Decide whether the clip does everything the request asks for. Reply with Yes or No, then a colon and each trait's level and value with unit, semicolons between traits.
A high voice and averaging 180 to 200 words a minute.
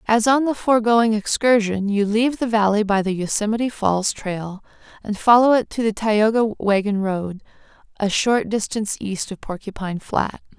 No: high, 215 Hz; average, 165 wpm